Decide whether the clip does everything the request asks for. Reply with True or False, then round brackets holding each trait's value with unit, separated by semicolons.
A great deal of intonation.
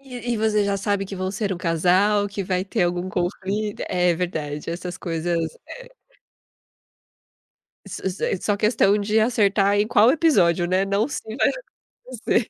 False (2.9 semitones)